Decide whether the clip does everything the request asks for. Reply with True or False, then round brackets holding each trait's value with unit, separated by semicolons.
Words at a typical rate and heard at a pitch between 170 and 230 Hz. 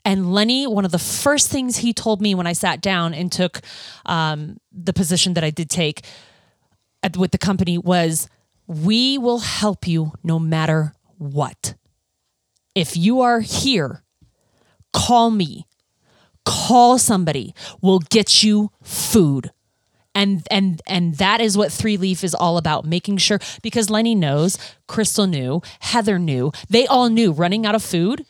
True (155 wpm; 185 Hz)